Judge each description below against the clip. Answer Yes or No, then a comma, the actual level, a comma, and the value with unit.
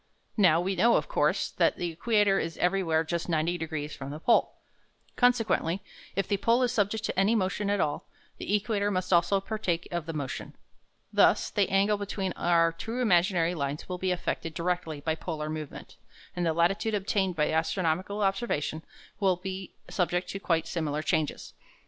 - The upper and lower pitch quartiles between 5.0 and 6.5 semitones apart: No, average, 3.6 semitones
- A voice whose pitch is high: No, medium, 180 Hz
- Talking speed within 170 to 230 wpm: Yes, average, 175 wpm